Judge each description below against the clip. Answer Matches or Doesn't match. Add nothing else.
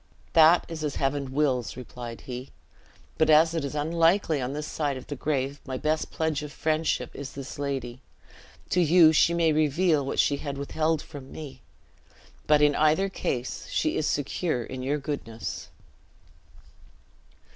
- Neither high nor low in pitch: Matches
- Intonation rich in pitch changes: Doesn't match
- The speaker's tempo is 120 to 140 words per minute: Doesn't match